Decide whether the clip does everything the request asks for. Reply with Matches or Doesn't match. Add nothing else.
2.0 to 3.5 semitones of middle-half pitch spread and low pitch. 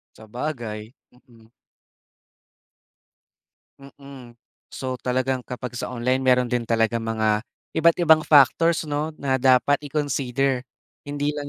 Matches